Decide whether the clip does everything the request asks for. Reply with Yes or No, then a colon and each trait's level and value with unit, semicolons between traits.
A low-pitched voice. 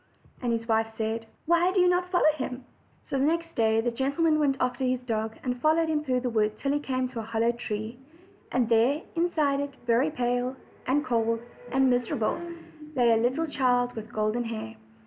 No: very high, 250 Hz